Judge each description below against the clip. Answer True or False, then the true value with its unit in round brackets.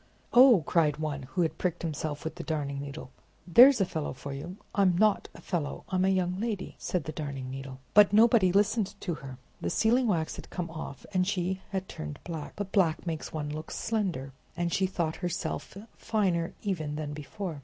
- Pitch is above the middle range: False (175 Hz)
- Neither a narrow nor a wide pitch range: True (4.4 semitones)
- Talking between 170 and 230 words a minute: True (195 wpm)